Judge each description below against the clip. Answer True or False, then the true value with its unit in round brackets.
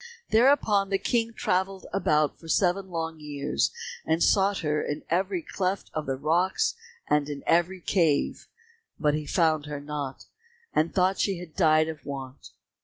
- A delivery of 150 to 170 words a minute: True (160 wpm)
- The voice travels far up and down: False (4.1 semitones)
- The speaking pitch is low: False (165 Hz)